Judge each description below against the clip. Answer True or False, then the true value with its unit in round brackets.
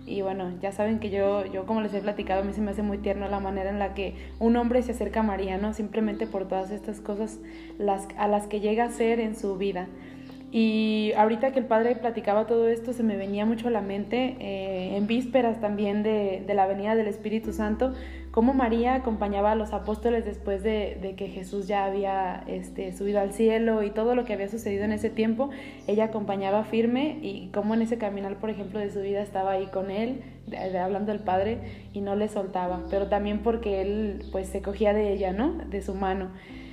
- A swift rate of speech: True (220 wpm)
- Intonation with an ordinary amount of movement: False (2.1 semitones)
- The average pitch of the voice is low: False (205 Hz)